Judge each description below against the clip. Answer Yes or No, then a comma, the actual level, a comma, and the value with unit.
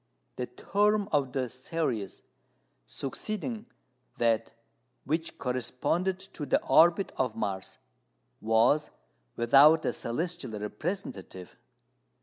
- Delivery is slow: Yes, slow, 95 wpm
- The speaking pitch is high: No, low, 135 Hz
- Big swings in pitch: Yes, wide, 7.2 semitones